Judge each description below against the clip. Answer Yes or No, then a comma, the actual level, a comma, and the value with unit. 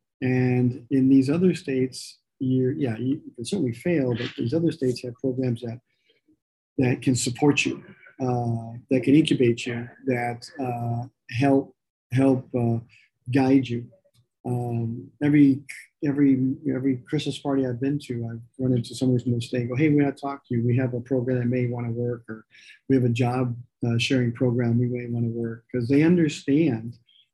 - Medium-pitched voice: No, low, 125 Hz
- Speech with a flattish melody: Yes, narrow, 2.3 semitones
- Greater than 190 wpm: No, average, 185 wpm